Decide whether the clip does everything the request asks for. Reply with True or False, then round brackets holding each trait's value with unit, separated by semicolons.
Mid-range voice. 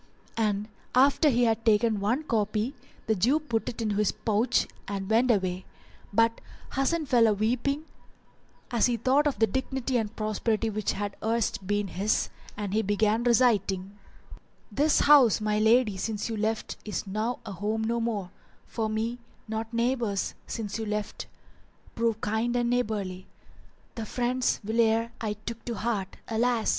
False (220 Hz)